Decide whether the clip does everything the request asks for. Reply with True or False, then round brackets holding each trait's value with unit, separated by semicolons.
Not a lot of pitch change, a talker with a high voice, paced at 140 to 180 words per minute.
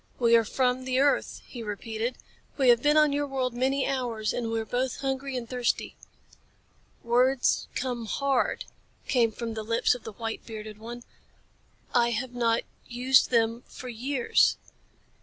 True (2.2 semitones; 245 Hz; 160 wpm)